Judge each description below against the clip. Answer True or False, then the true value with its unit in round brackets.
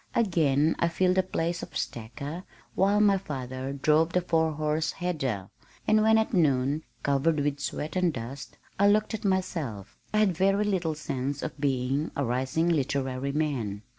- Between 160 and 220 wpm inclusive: True (165 wpm)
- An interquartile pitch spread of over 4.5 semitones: True (5.1 semitones)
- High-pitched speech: False (155 Hz)